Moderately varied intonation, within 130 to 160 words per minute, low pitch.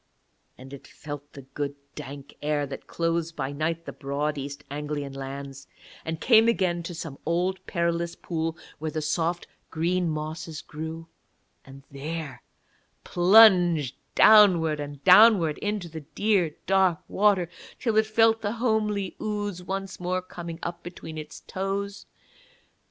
No: average, 4.3 semitones; average, 140 wpm; medium, 165 Hz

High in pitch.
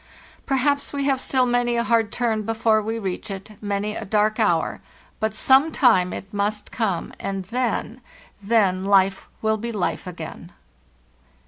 Yes: high, 215 Hz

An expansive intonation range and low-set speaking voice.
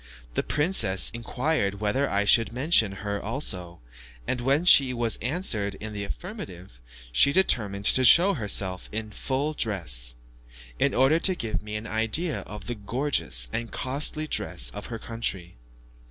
Yes: wide, 5.7 semitones; low, 115 Hz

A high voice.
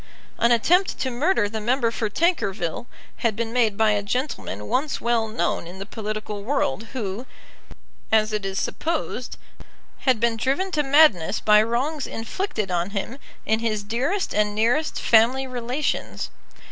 Yes: high, 230 Hz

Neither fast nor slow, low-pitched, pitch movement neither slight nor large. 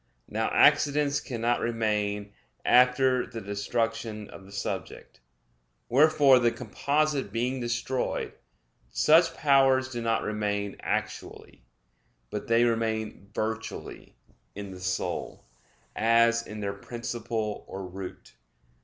No: slow, 110 wpm; low, 115 Hz; average, 3.5 semitones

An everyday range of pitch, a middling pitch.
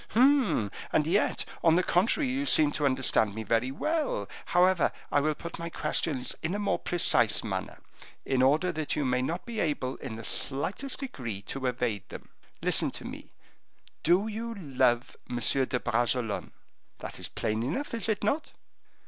No: wide, 8.3 semitones; medium, 150 Hz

